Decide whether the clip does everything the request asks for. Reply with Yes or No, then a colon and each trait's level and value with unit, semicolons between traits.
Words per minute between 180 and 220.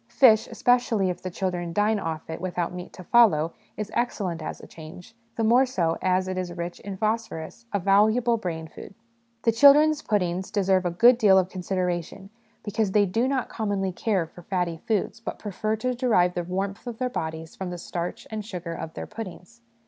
Yes: average, 195 wpm